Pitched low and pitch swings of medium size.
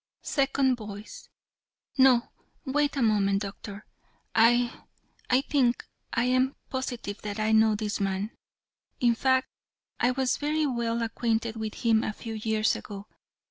No: high, 230 Hz; average, 3.2 semitones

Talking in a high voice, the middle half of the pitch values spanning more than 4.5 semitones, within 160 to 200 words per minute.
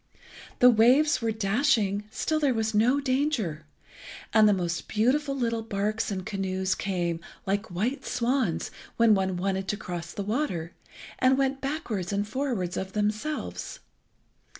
No: high, 215 Hz; average, 5.1 semitones; average, 145 wpm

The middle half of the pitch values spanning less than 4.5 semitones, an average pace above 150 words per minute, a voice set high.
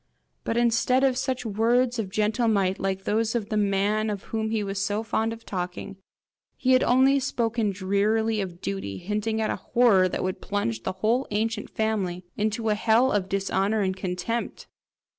Yes: average, 2.8 semitones; average, 180 wpm; high, 215 Hz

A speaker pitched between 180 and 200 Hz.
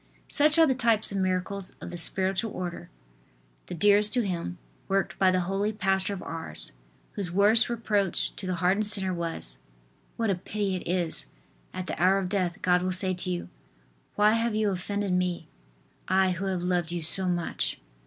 Yes: high, 190 Hz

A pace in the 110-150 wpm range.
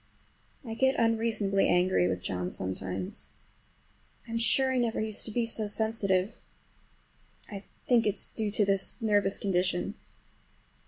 Yes: average, 140 wpm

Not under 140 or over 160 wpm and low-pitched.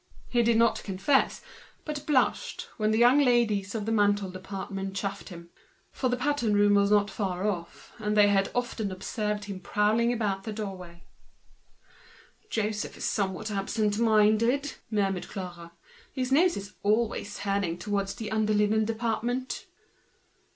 No: average, 155 wpm; high, 210 Hz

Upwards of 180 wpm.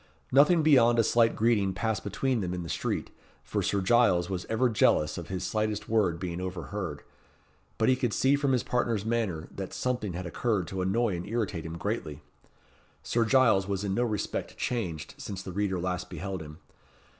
Yes: average, 190 wpm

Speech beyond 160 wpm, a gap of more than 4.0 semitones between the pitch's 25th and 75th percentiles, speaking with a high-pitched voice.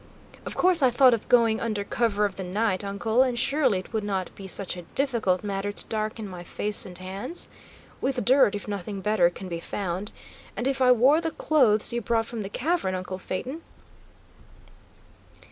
Yes: average, 190 wpm; average, 4.5 semitones; high, 215 Hz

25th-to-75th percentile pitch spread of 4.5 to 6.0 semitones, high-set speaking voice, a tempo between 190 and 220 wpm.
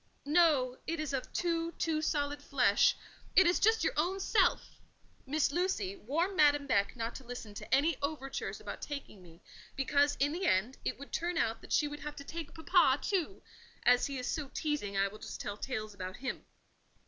Yes: average, 4.9 semitones; very high, 285 Hz; average, 195 wpm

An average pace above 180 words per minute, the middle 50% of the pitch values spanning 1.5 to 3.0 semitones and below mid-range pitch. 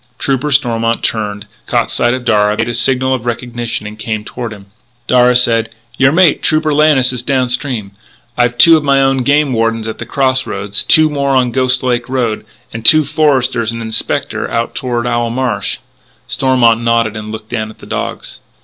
Yes: average, 195 wpm; narrow, 2.6 semitones; low, 120 Hz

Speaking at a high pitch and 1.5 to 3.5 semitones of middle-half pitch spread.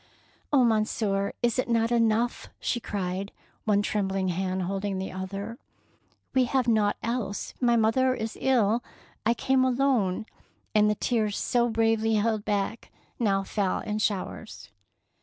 Yes: high, 220 Hz; average, 3.0 semitones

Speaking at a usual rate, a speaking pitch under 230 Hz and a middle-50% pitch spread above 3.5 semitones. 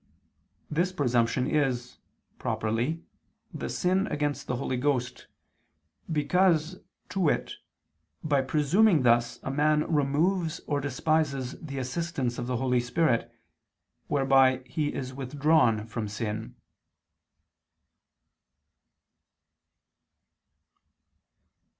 No: slow, 90 wpm; medium, 140 Hz; average, 3.9 semitones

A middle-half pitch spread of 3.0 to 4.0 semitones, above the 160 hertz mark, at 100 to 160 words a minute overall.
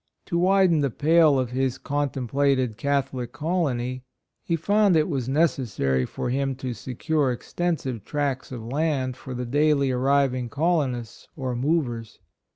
No: average, 3.6 semitones; low, 135 Hz; average, 150 wpm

